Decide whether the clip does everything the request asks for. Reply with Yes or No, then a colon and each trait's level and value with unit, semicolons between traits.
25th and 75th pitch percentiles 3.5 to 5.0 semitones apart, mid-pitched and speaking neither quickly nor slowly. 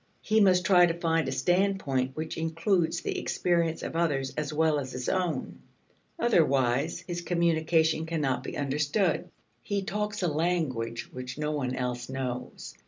Yes: average, 4.7 semitones; medium, 160 Hz; average, 155 wpm